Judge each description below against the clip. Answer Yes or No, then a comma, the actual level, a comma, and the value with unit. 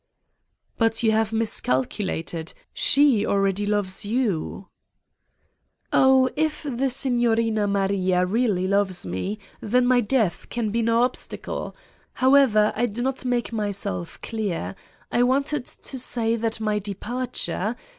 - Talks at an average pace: No, slow, 125 wpm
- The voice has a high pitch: Yes, high, 225 Hz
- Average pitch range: Yes, average, 3.7 semitones